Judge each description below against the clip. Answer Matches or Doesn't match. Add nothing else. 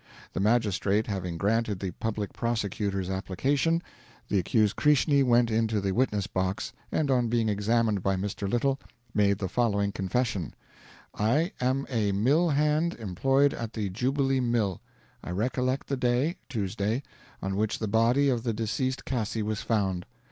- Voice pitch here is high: Doesn't match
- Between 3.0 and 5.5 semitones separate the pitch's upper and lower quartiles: Matches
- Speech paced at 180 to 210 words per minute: Doesn't match